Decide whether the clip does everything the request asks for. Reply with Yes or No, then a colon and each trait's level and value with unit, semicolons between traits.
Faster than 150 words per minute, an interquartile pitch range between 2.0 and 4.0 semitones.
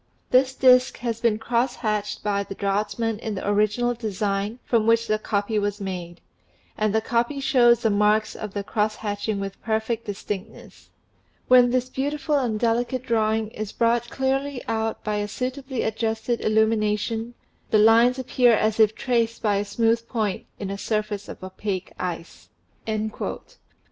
Yes: average, 160 wpm; narrow, 2.4 semitones